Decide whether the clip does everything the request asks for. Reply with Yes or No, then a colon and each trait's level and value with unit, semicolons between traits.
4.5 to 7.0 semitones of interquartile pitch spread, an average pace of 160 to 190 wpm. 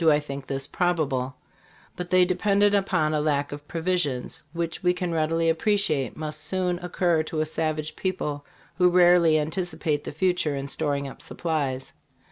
No: average, 3.2 semitones; average, 165 wpm